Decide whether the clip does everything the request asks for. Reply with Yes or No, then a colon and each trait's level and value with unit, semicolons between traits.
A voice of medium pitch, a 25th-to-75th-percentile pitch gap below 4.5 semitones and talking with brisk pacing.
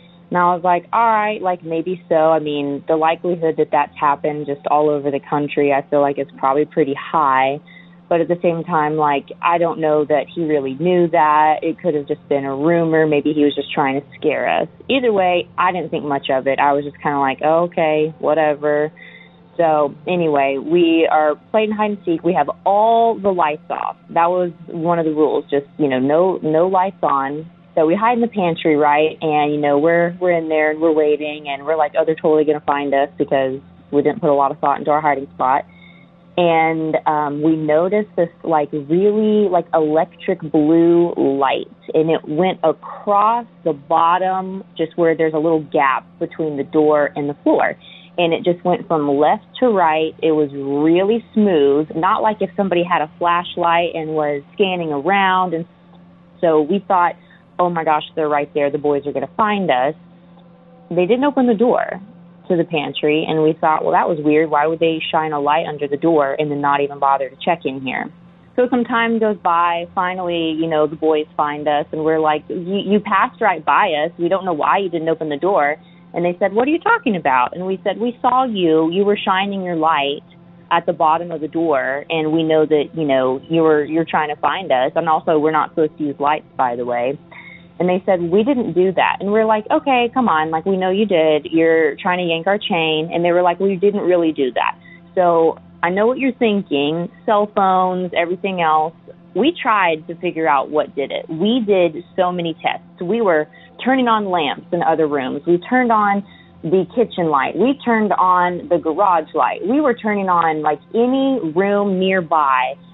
Yes: medium, 165 Hz; average, 3.3 semitones; fast, 215 wpm